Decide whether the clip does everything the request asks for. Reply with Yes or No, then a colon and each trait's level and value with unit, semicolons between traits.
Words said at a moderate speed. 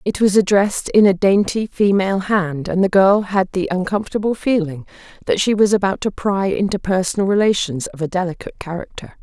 Yes: average, 180 wpm